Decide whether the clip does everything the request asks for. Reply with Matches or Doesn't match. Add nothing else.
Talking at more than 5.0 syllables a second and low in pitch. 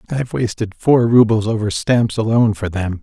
Matches